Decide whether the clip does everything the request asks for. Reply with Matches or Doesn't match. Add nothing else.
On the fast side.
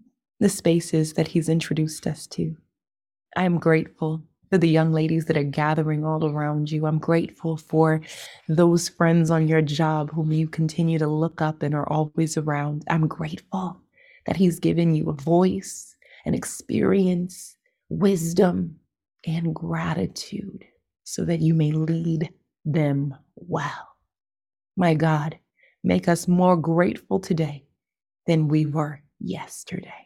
Doesn't match